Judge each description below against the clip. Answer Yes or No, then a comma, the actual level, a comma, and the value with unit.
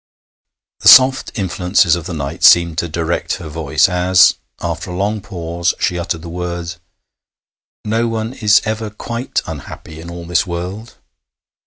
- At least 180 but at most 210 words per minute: No, average, 155 wpm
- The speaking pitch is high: No, very low, 90 Hz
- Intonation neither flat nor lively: Yes, average, 3.7 semitones